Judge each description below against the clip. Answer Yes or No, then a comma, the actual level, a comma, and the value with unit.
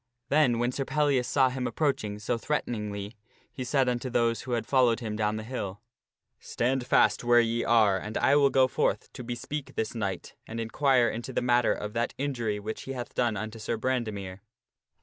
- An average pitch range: Yes, average, 3.0 semitones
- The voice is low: Yes, low, 120 Hz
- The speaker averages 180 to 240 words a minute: Yes, average, 200 wpm